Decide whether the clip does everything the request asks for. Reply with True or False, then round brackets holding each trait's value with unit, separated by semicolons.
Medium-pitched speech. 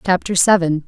True (180 Hz)